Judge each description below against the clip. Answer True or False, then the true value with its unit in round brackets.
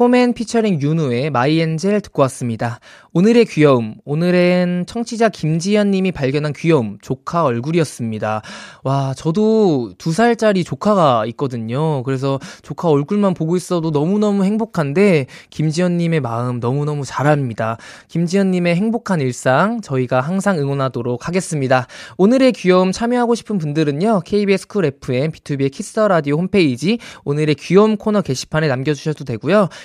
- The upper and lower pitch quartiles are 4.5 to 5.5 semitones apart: False (6.6 semitones)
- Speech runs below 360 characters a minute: False (365 characters per minute)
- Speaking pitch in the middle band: True (160 Hz)